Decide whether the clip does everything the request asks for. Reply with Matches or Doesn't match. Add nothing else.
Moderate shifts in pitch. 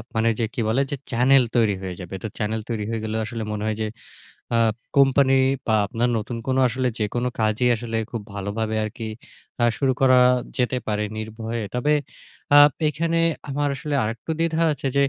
Matches